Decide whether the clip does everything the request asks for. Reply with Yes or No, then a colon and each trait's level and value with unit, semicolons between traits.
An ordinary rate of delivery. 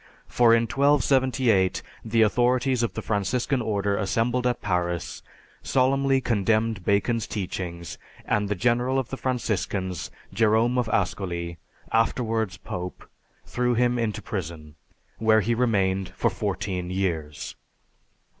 No: slow, 120 wpm